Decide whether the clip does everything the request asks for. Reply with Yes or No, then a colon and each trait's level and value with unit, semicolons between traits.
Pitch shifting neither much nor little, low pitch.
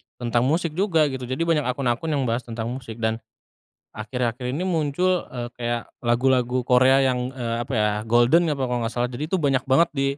Yes: average, 3.5 semitones; low, 125 Hz